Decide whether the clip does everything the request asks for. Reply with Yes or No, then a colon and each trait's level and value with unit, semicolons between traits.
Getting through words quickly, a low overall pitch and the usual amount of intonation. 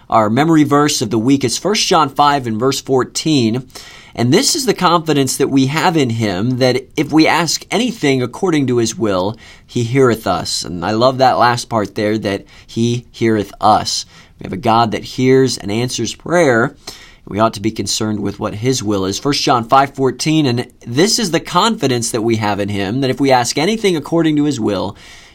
Yes: fast, 210 wpm; low, 125 Hz; average, 4.7 semitones